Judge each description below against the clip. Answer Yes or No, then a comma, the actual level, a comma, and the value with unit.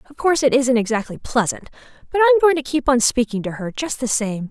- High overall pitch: Yes, very high, 255 Hz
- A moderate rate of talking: No, fast, 240 wpm